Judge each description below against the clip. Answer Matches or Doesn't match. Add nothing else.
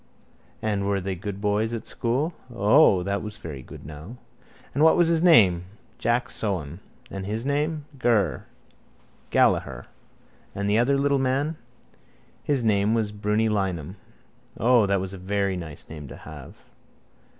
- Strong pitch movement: Doesn't match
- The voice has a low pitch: Matches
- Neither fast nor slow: Matches